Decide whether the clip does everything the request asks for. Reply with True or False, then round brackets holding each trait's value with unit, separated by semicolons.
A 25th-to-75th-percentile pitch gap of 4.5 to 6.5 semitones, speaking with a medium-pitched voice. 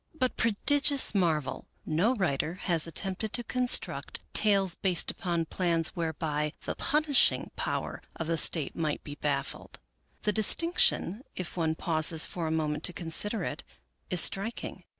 True (4.8 semitones; 175 Hz)